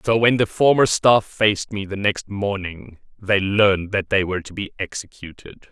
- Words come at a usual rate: Yes, average, 190 wpm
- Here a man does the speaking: Yes, male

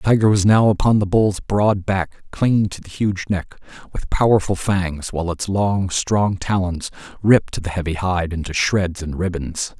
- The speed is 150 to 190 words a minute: Yes, average, 185 wpm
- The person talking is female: No, male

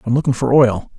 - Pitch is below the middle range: Yes, low, 125 Hz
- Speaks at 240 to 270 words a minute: Yes, fast, 245 wpm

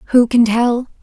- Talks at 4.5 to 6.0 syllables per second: No, 3.5 syllables/s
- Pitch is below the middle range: No, high, 235 Hz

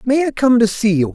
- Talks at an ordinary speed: No, fast, 315 wpm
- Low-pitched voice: No, high, 230 Hz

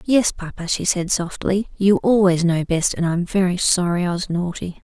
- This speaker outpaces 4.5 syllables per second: Yes, 4.9 syllables/s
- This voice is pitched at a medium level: Yes, medium, 180 Hz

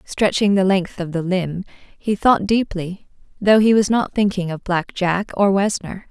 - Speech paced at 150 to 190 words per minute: Yes, average, 185 wpm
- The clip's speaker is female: Yes, female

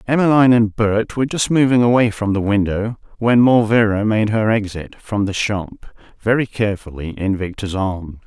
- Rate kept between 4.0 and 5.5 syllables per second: Yes, 5.0 syllables/s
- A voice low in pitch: Yes, low, 110 Hz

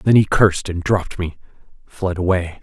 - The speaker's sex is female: No, male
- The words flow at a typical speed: Yes, average, 185 wpm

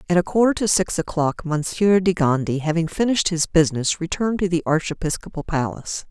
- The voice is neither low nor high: Yes, medium, 170 Hz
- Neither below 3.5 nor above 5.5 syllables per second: No, 5.9 syllables/s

